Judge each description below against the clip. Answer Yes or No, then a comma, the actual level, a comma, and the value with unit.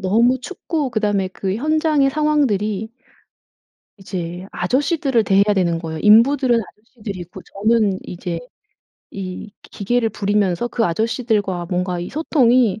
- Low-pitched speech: No, high, 210 Hz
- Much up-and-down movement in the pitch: No, average, 5.0 semitones